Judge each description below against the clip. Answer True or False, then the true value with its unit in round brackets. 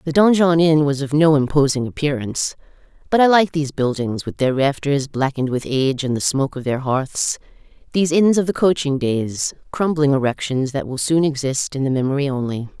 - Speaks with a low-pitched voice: False (145 Hz)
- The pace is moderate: True (190 wpm)